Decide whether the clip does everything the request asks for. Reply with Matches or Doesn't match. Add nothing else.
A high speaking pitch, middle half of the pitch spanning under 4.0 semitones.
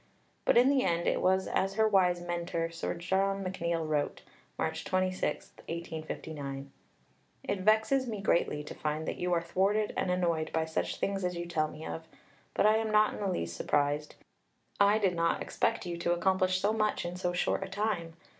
Doesn't match